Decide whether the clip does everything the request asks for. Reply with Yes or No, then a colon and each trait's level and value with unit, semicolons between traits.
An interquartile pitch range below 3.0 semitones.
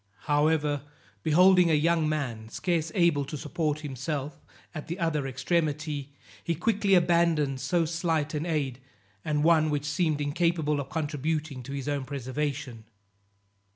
Yes: narrow, 2.6 semitones